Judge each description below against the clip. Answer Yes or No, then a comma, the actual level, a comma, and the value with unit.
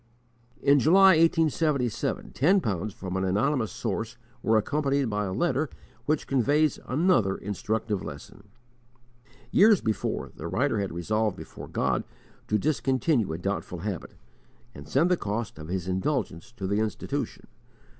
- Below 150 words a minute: Yes, average, 140 wpm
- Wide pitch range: Yes, wide, 7.0 semitones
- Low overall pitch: Yes, low, 110 Hz